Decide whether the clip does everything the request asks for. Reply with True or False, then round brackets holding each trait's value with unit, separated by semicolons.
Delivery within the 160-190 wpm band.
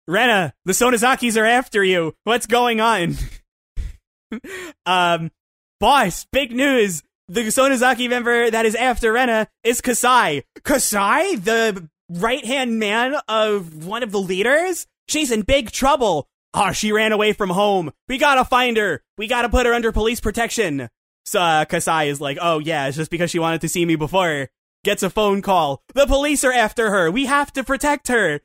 True (180 wpm)